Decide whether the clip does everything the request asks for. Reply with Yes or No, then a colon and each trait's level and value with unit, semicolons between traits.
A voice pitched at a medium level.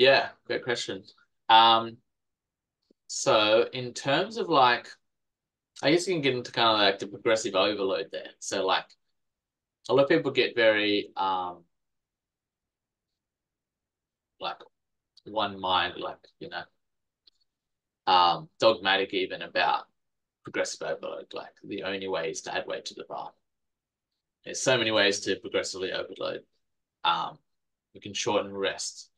No: low, 100 Hz